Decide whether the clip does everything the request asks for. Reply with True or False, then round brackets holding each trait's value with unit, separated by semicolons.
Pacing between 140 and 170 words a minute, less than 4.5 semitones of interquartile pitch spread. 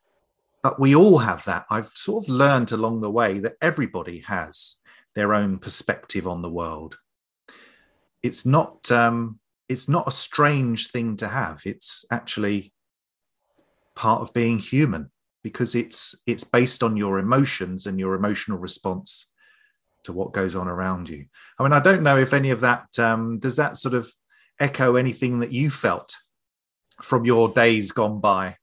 False (165 wpm; 4.8 semitones)